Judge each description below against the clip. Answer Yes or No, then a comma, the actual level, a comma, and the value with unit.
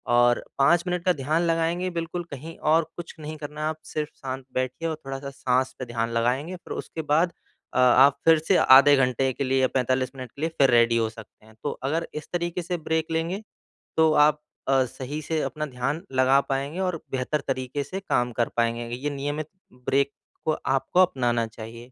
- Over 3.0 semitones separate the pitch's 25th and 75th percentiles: Yes, average, 4.0 semitones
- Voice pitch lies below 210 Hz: Yes, medium, 140 Hz